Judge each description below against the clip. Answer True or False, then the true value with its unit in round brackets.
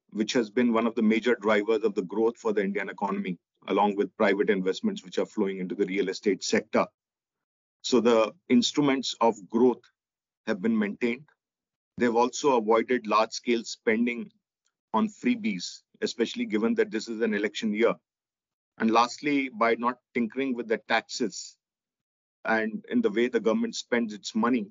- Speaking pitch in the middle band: False (120 Hz)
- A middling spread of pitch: False (5.8 semitones)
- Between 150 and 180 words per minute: True (165 wpm)